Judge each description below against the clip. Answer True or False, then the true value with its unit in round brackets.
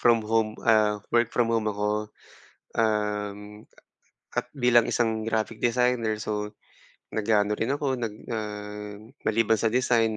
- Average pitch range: False (1.7 semitones)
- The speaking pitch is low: True (110 Hz)